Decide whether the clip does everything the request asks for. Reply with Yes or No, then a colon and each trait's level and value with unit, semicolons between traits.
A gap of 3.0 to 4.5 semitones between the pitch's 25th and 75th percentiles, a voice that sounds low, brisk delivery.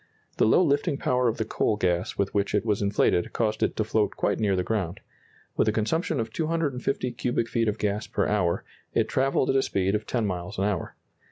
Yes: average, 3.8 semitones; low, 110 Hz; fast, 225 wpm